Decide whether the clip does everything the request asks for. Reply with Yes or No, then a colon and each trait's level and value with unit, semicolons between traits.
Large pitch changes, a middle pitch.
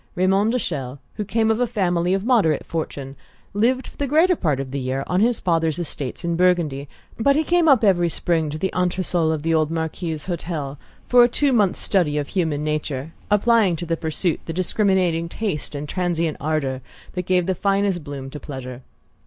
No: average, 4.8 semitones; medium, 170 Hz